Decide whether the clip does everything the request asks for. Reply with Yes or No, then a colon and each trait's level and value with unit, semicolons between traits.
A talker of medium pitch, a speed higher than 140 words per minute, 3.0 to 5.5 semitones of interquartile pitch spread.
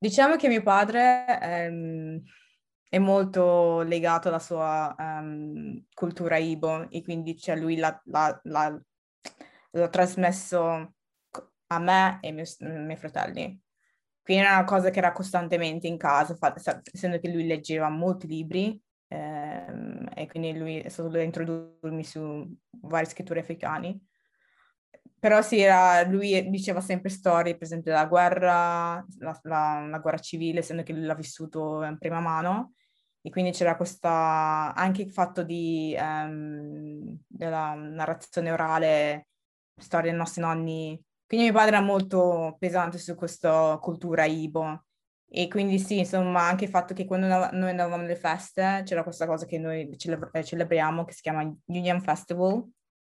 No: medium, 170 Hz; average, 150 wpm; narrow, 2.5 semitones